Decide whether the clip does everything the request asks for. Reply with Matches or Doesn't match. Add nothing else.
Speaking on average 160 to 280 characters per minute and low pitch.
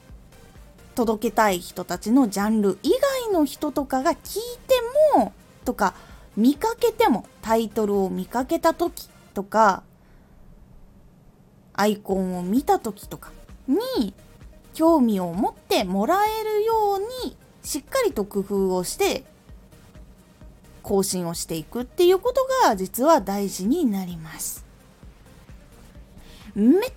Doesn't match